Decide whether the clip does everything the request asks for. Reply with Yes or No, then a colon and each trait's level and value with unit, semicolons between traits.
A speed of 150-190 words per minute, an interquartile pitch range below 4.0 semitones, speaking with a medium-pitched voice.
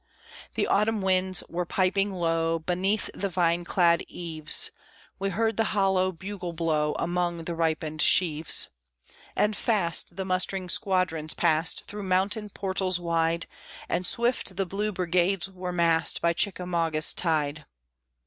No: slow, 135 wpm; narrow, 2.6 semitones; medium, 180 Hz